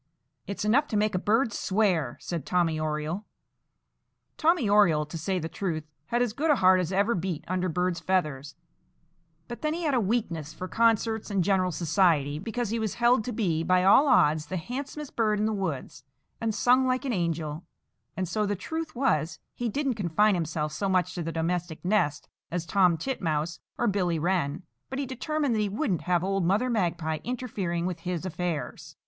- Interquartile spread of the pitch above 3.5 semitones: Yes, average, 5.2 semitones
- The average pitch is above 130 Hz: Yes, medium, 185 Hz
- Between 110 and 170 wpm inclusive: No, average, 190 wpm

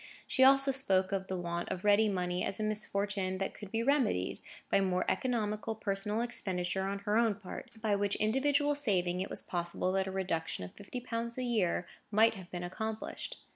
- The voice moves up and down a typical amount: Yes, average, 3.5 semitones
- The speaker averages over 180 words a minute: Yes, average, 195 wpm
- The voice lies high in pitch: Yes, high, 205 Hz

